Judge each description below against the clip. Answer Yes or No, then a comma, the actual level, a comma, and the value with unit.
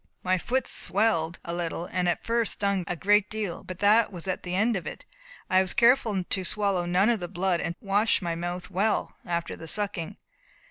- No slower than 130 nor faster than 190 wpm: No, fast, 205 wpm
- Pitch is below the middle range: No, high, 190 Hz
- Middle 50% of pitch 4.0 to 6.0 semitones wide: No, average, 2.9 semitones